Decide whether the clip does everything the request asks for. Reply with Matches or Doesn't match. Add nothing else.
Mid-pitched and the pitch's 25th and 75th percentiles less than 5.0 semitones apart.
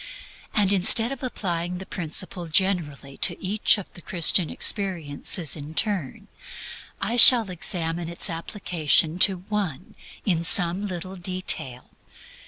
Matches